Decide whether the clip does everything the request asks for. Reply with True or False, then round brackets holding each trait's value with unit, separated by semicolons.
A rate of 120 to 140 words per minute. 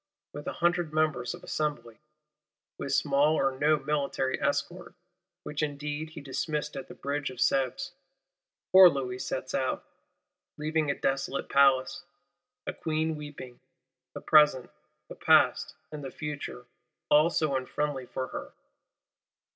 True (135 wpm)